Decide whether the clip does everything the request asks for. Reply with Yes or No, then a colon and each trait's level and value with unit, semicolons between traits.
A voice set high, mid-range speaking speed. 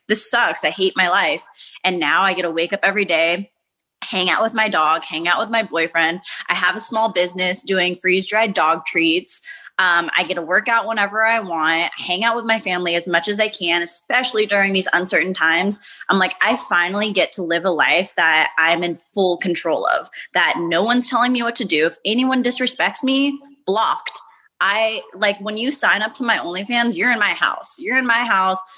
No: high, 195 Hz; fast, 215 wpm